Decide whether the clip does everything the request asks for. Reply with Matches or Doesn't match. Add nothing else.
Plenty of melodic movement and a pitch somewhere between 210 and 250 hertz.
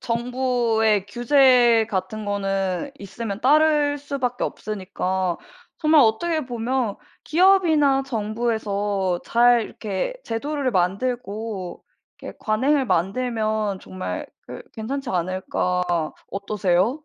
Doesn't match